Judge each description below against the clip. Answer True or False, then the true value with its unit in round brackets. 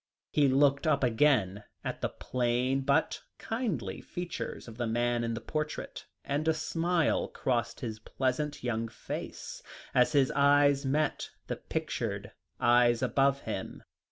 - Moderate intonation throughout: True (3.7 semitones)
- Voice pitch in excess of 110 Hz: True (135 Hz)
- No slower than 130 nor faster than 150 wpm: True (140 wpm)